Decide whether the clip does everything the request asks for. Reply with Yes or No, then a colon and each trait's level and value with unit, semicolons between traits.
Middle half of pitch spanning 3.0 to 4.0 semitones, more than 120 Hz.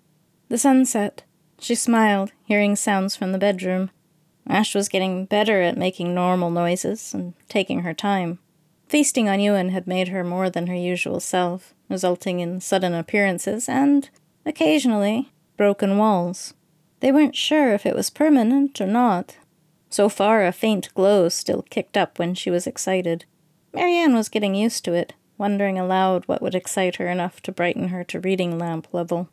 Yes: average, 3.3 semitones; high, 190 Hz